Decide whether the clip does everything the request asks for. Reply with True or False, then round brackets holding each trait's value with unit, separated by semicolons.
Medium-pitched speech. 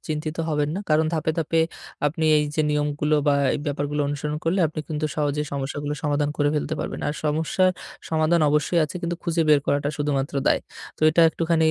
True (150 Hz)